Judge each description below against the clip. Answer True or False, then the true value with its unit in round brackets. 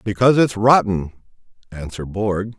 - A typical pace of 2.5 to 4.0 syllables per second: False (5.3 syllables/s)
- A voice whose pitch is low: True (105 Hz)